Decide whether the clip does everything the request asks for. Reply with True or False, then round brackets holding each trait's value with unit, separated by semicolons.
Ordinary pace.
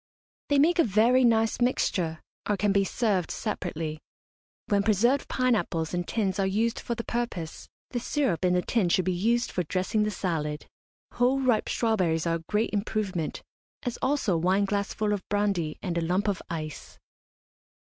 True (175 wpm)